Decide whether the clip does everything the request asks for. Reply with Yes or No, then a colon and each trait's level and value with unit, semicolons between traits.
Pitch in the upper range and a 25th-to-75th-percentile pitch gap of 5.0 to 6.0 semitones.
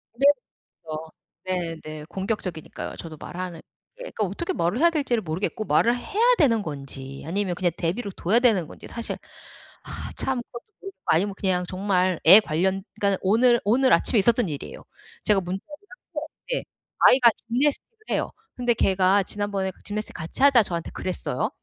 Yes: high, 195 Hz; average, 5.3 semitones